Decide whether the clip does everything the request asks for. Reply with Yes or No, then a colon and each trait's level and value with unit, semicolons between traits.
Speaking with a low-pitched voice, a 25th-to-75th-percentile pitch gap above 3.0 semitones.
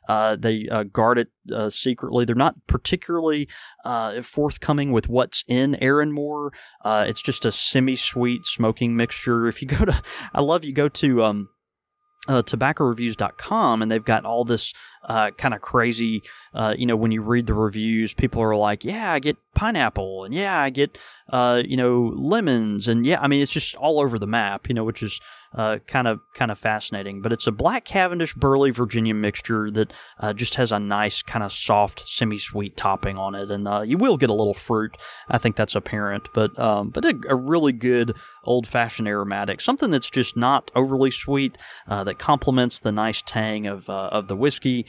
Yes: low, 115 Hz; average, 3.7 semitones